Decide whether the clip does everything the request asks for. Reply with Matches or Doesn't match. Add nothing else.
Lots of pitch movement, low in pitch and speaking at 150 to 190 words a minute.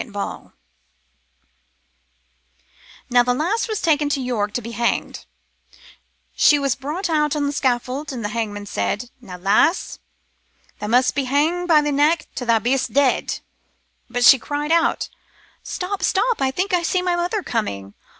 Doesn't match